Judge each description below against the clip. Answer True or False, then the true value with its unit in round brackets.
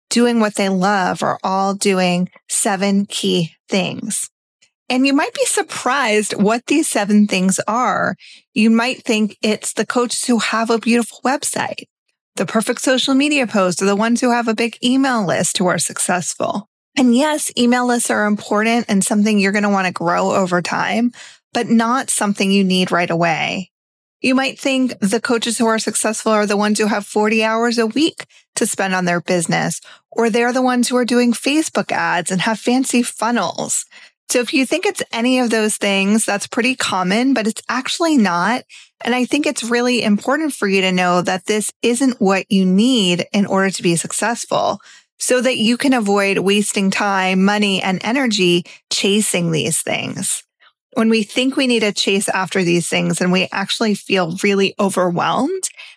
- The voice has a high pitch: True (215 Hz)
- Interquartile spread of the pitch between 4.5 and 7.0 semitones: False (4.0 semitones)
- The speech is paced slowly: False (185 wpm)